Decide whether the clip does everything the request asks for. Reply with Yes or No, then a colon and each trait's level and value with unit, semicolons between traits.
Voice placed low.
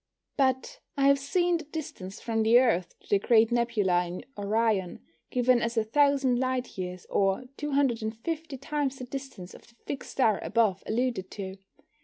No: high, 235 Hz